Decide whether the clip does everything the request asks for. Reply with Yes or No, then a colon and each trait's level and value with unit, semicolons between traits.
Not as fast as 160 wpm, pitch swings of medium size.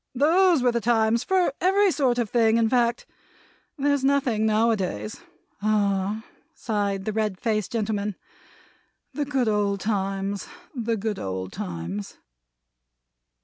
Yes: slow, 135 wpm; average, 3.7 semitones